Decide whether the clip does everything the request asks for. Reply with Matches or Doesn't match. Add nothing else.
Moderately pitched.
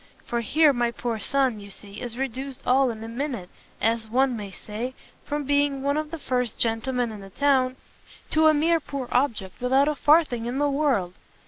Doesn't match